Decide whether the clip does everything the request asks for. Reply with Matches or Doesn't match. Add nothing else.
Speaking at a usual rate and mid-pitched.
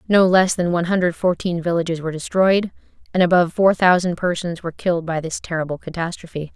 Matches